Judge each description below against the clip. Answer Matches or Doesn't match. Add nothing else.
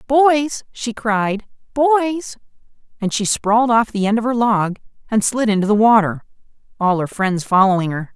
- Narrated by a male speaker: Doesn't match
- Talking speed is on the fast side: Doesn't match